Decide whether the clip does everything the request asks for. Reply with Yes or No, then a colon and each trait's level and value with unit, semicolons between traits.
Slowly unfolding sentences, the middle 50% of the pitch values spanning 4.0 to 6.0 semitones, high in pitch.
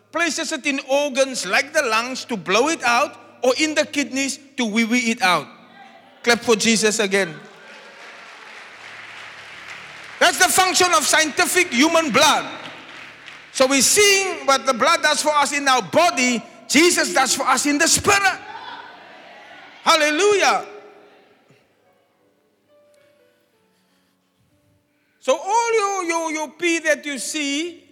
Yes: slow, 130 wpm; average, 4.3 semitones; very high, 295 Hz